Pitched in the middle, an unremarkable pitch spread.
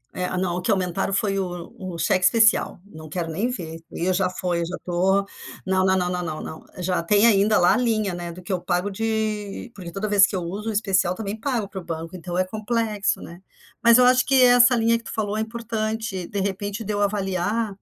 No: high, 195 Hz; average, 3.4 semitones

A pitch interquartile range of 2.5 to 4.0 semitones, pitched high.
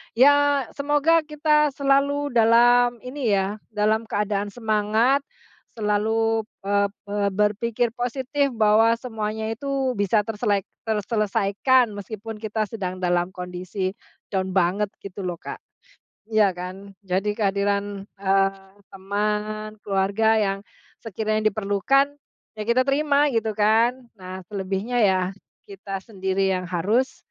Yes: average, 3.5 semitones; high, 215 Hz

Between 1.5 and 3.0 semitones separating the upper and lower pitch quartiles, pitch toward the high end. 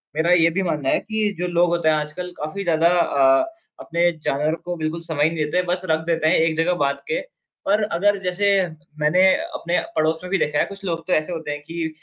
No: narrow, 2.5 semitones; medium, 165 Hz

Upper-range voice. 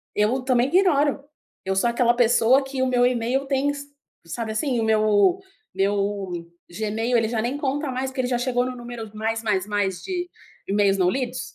Yes: high, 240 Hz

